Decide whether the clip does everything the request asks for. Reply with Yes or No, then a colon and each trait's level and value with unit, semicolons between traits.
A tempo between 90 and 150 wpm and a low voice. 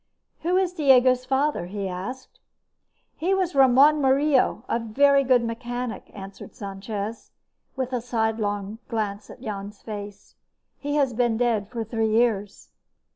No: average, 140 wpm; high, 235 Hz